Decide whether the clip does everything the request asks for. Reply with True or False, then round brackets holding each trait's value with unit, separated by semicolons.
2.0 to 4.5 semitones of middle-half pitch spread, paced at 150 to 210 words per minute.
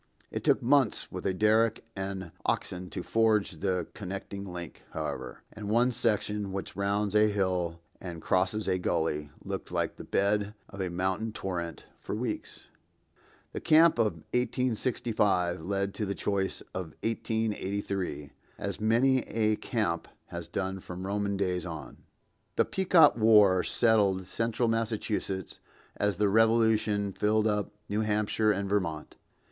False (2.8 semitones; 140 wpm)